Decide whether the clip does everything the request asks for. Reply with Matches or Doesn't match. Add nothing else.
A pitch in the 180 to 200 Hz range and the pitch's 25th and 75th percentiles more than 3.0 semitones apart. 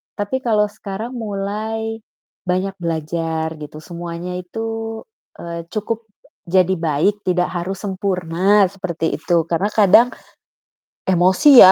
Matches